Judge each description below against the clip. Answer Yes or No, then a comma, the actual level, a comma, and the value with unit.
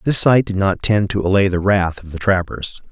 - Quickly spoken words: Yes, fast, 245 wpm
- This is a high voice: No, very low, 95 Hz